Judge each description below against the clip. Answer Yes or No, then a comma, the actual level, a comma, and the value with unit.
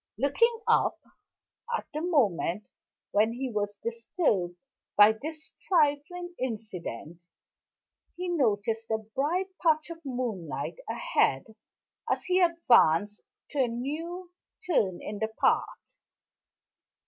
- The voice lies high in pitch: Yes, very high, 250 Hz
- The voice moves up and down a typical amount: No, wide, 8.2 semitones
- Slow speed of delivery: Yes, slow, 110 wpm